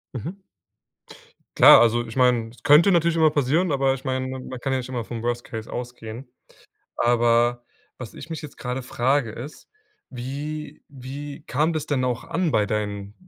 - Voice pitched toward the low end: Yes, low, 130 Hz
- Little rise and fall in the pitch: No, average, 3.4 semitones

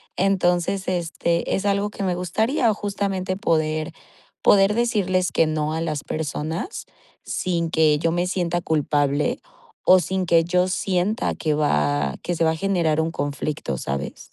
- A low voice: No, medium, 170 Hz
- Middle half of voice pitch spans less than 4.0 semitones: Yes, average, 3.4 semitones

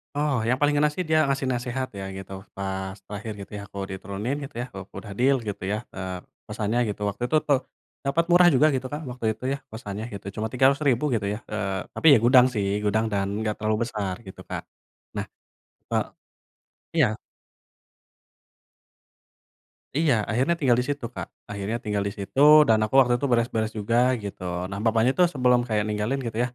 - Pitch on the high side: No, low, 115 Hz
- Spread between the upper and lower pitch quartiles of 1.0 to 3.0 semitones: No, average, 4.5 semitones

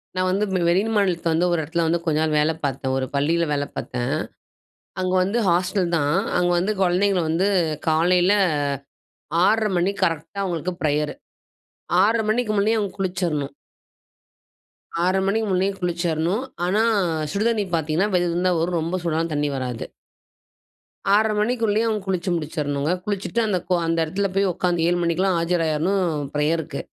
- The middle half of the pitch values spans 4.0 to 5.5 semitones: No, average, 3.6 semitones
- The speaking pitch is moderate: Yes, medium, 175 Hz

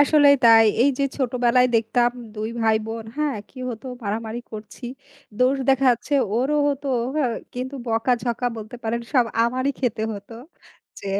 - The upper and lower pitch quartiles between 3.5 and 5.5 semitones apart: No, average, 2.9 semitones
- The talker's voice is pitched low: No, high, 240 Hz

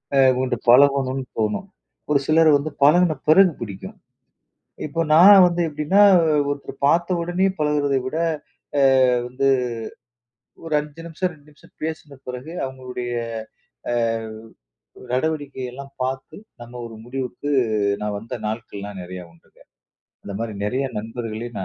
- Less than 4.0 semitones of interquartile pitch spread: No, average, 4.3 semitones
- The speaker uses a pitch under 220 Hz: Yes, low, 135 Hz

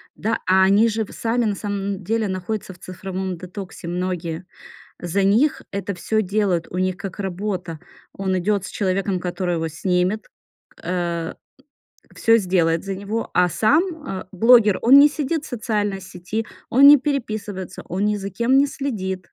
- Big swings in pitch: No, average, 3.3 semitones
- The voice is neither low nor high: No, high, 195 Hz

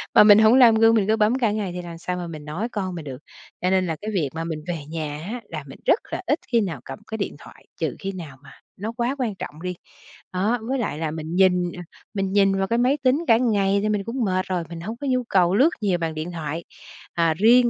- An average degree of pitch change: Yes, average, 4.8 semitones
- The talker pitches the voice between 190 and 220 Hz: Yes, high, 195 Hz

